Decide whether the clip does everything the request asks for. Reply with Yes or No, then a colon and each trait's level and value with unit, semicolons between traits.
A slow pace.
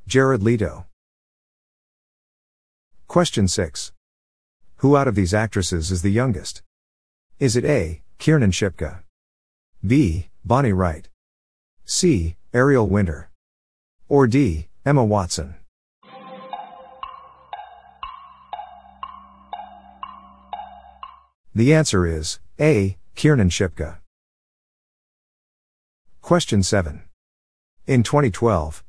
Yes: slow, 75 wpm